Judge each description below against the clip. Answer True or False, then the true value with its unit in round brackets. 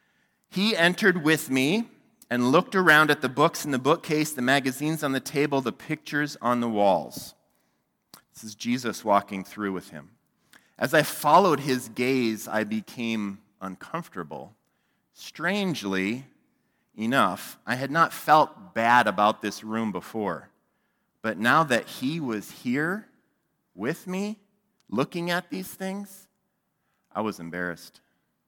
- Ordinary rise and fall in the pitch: False (7.9 semitones)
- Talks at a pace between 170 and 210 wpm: False (135 wpm)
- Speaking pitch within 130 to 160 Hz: True (135 Hz)